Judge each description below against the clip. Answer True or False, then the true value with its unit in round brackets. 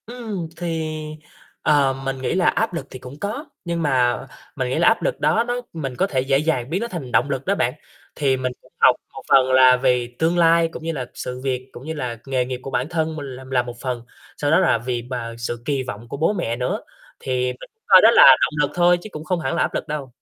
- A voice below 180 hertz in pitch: True (135 Hz)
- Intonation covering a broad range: False (4.7 semitones)